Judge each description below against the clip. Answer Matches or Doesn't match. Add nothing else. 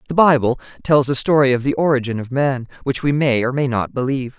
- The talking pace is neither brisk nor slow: Doesn't match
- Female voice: Matches